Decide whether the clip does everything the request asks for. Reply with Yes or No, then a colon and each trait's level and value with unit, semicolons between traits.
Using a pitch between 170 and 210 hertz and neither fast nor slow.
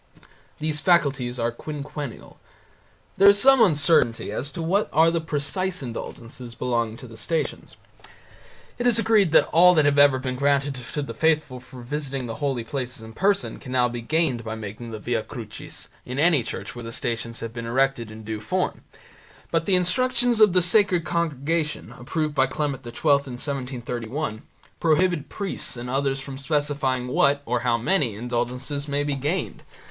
No: medium, 140 Hz; average, 175 wpm